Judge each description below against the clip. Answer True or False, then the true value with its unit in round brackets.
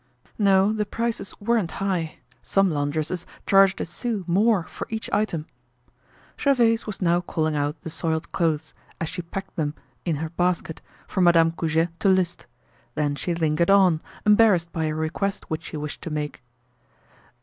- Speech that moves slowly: False (160 wpm)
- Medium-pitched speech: True (170 Hz)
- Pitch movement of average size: True (3.8 semitones)